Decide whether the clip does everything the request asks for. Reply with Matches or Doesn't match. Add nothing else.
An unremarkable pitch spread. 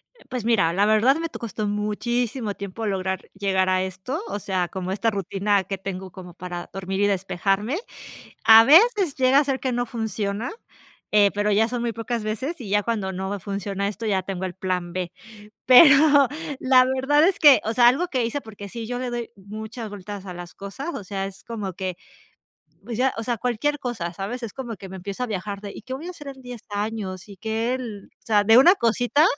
Matches